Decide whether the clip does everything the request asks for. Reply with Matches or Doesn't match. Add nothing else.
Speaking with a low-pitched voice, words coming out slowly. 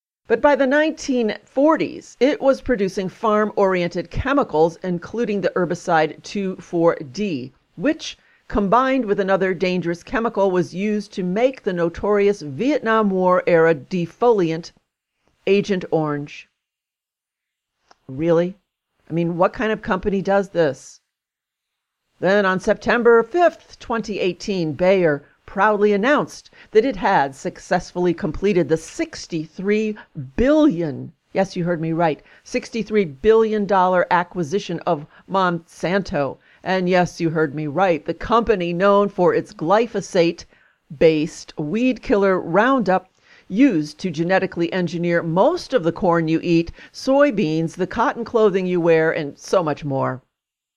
Doesn't match